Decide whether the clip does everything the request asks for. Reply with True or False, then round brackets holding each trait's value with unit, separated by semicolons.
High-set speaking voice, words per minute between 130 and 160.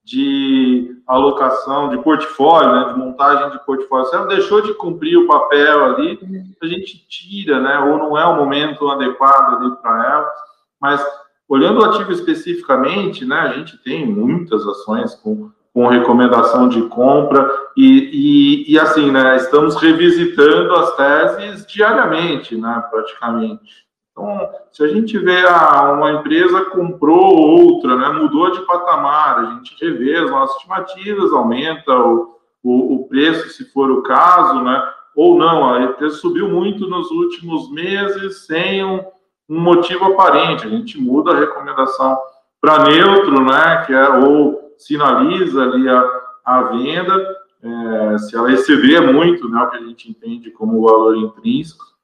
False (165 Hz; 150 wpm)